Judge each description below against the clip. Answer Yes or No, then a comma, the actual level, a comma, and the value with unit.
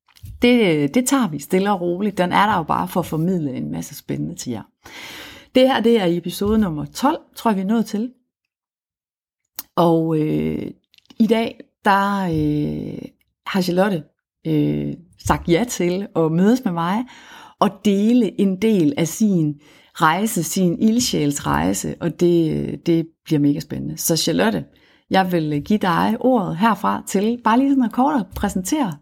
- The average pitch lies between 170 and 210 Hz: Yes, medium, 185 Hz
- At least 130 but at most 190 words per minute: Yes, average, 165 wpm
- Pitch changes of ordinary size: No, wide, 5.9 semitones